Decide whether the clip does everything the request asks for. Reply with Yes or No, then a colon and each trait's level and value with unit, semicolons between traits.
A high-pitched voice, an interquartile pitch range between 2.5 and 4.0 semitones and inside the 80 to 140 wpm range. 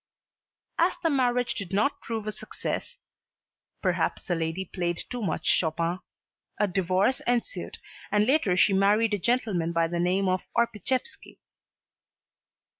No: high, 200 Hz; average, 4.9 semitones; slow, 135 wpm